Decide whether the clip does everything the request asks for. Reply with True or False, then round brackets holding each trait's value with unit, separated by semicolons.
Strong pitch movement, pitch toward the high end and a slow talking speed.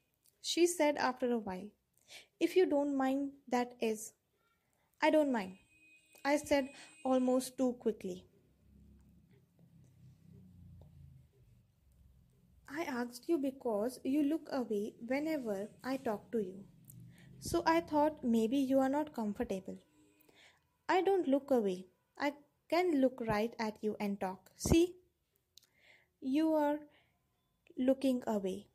True (7.3 semitones; 240 Hz; 115 wpm)